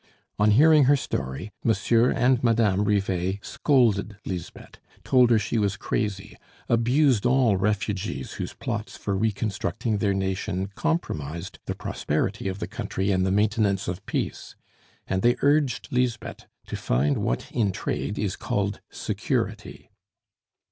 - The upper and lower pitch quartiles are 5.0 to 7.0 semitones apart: No, average, 3.8 semitones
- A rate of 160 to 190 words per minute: No, slow, 135 wpm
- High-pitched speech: No, low, 105 Hz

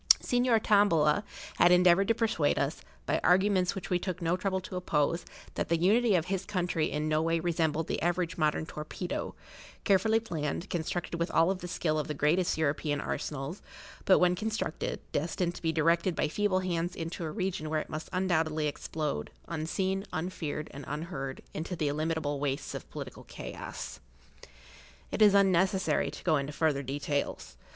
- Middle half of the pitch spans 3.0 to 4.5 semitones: Yes, average, 3.3 semitones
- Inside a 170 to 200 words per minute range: Yes, average, 175 wpm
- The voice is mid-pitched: Yes, medium, 170 Hz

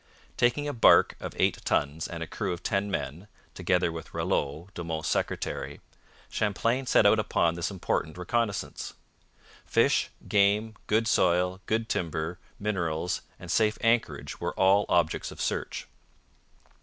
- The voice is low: Yes, very low, 95 Hz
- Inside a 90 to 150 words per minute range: Yes, average, 145 wpm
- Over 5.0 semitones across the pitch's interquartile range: No, average, 4.0 semitones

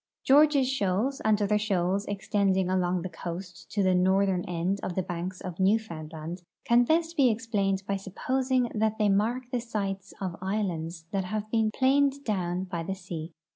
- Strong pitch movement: No, average, 3.5 semitones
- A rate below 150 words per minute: No, average, 175 wpm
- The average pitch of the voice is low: No, high, 195 Hz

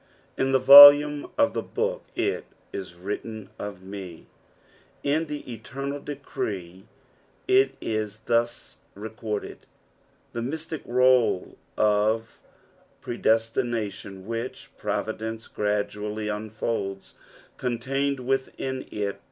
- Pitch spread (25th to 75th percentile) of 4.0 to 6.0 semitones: Yes, average, 4.3 semitones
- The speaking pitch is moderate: No, low, 115 Hz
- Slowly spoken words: Yes, slow, 100 wpm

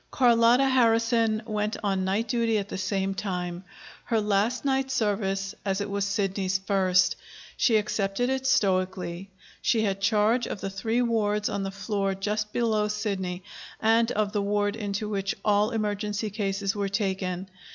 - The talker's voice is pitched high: Yes, high, 205 Hz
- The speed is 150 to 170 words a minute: Yes, average, 160 wpm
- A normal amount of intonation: No, narrow, 2.3 semitones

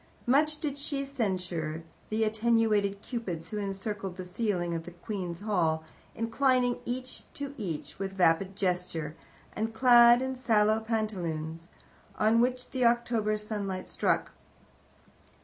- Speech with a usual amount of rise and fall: Yes, average, 4.8 semitones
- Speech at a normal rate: No, slow, 130 wpm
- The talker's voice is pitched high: Yes, high, 215 Hz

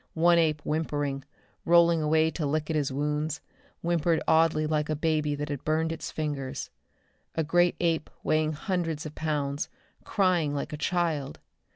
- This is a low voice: No, medium, 155 Hz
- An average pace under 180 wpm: Yes, average, 160 wpm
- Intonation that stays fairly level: Yes, narrow, 1.8 semitones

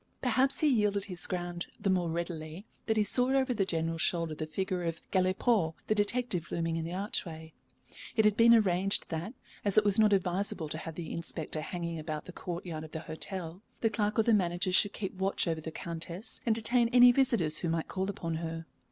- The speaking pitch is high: No, medium, 180 Hz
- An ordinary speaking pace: No, fast, 210 wpm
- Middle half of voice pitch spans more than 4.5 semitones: No, average, 4.2 semitones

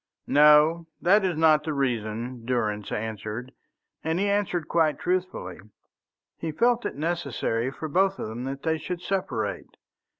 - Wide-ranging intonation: Yes, wide, 6.3 semitones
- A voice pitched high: No, medium, 150 Hz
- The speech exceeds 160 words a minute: No, average, 145 wpm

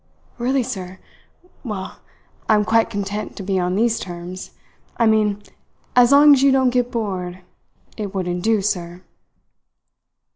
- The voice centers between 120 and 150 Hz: No, high, 210 Hz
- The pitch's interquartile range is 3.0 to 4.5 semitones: Yes, average, 4.2 semitones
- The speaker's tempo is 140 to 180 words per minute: Yes, average, 145 wpm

